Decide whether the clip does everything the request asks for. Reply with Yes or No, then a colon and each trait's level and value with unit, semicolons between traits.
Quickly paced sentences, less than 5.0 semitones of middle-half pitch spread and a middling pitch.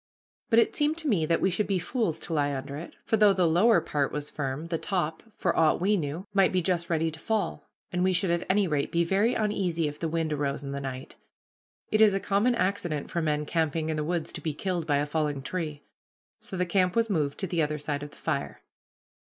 Yes: fast, 245 wpm; average, 4.3 semitones; medium, 170 Hz